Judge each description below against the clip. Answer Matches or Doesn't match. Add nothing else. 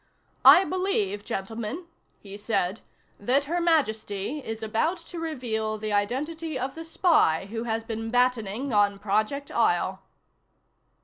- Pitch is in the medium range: Doesn't match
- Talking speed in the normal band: Doesn't match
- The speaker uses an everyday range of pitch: Doesn't match